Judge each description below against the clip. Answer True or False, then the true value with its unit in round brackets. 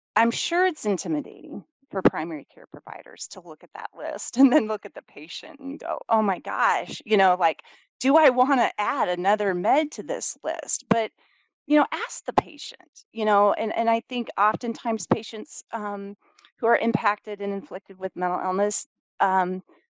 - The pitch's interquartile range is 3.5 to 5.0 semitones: True (3.9 semitones)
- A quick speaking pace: False (180 wpm)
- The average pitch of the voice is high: True (215 Hz)